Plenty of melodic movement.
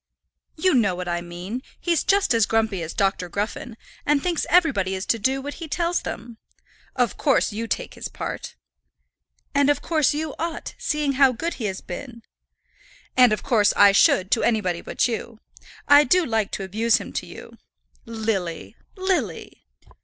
Yes: wide, 6.4 semitones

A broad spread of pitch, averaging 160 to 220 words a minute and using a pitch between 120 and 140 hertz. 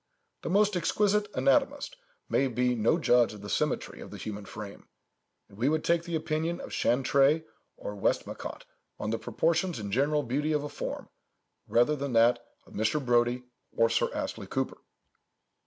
Yes: wide, 5.8 semitones; average, 170 wpm; low, 135 Hz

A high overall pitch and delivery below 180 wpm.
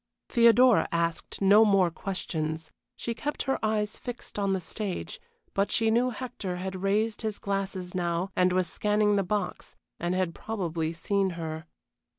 Yes: high, 195 Hz; average, 160 wpm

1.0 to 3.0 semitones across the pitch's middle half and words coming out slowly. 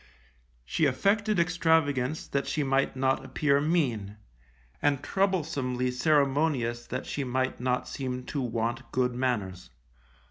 No: average, 3.4 semitones; slow, 120 wpm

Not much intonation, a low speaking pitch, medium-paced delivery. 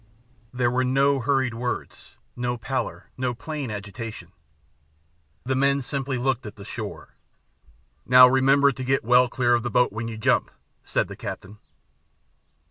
Yes: narrow, 2.3 semitones; low, 125 Hz; average, 150 wpm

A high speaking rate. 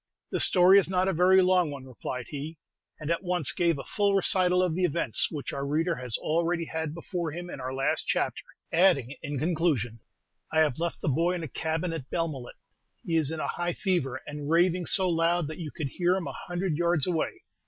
Yes: fast, 215 wpm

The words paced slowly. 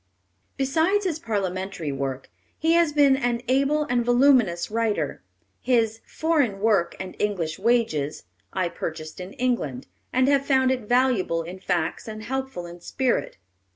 No: average, 145 wpm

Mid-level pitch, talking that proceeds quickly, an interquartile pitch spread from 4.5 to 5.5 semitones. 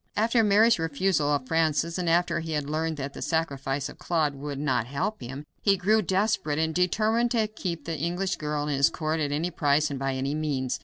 No: medium, 160 Hz; fast, 215 wpm; average, 4.0 semitones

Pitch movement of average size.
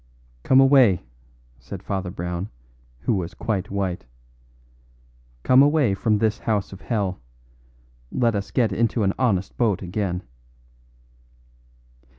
Yes: average, 3.8 semitones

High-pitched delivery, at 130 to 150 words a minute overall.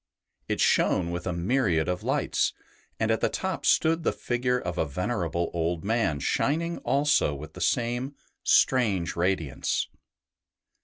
No: very low, 95 Hz; average, 145 wpm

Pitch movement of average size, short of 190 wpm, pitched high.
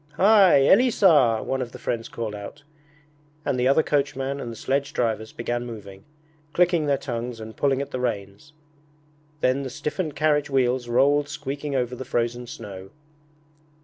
No: average, 3.7 semitones; average, 160 wpm; low, 130 Hz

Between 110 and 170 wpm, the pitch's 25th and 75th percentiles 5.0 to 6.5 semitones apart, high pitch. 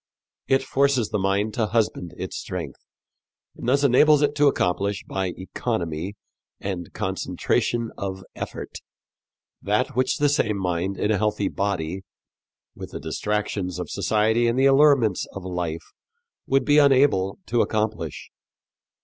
No: average, 140 wpm; average, 5.3 semitones; low, 105 Hz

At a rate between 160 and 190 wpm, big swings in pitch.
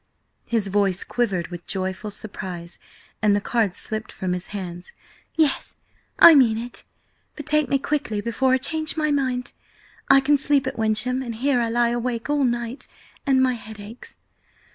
No: average, 170 wpm; average, 4.5 semitones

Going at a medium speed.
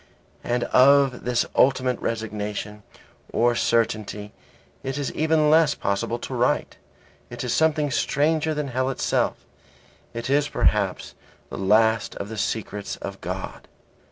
No: slow, 130 wpm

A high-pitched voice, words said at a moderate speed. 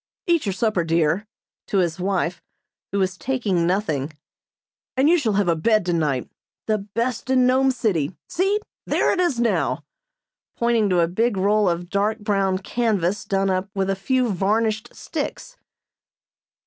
Yes: high, 200 Hz; average, 160 wpm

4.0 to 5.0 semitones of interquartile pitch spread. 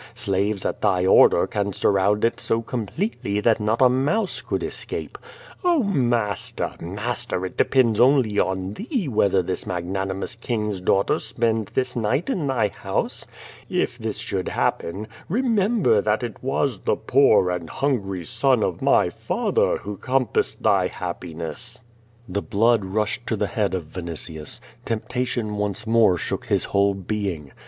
Yes: average, 4.4 semitones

